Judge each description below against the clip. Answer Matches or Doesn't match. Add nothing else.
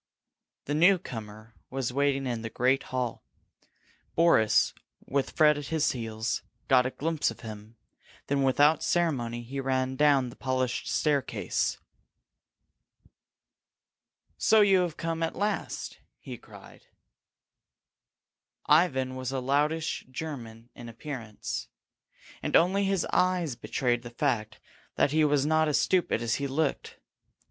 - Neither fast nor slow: Doesn't match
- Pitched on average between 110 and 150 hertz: Matches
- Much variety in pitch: Doesn't match